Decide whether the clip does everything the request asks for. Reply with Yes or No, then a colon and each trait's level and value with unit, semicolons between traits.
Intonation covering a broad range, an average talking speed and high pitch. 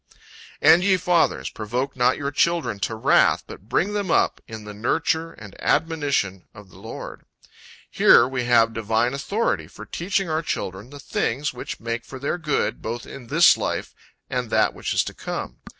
No: wide, 6.5 semitones; average, 180 wpm; low, 125 Hz